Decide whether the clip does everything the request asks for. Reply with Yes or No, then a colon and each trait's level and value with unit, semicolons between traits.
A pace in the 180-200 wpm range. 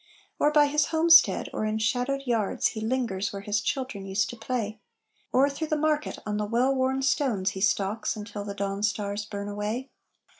Yes: average, 190 wpm